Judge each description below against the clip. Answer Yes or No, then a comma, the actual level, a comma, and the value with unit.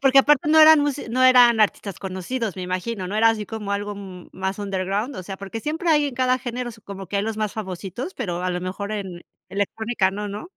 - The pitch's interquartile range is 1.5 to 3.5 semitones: No, average, 4.7 semitones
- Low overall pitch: No, high, 210 Hz